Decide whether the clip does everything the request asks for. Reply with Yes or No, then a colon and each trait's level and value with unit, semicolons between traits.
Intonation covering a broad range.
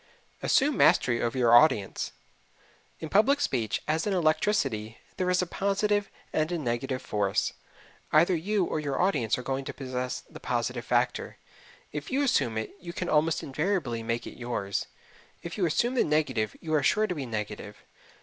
Yes: wide, 7.3 semitones